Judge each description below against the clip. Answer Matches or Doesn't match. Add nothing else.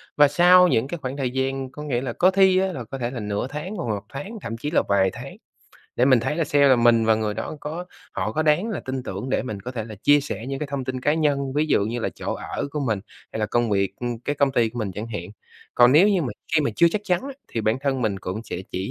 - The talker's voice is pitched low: Matches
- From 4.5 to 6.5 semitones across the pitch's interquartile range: Matches